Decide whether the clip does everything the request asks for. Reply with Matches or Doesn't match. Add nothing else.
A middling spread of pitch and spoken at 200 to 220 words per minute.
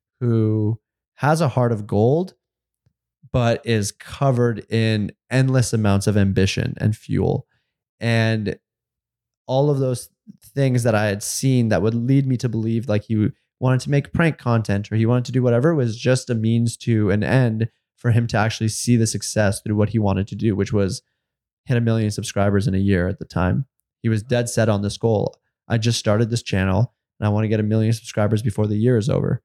Matches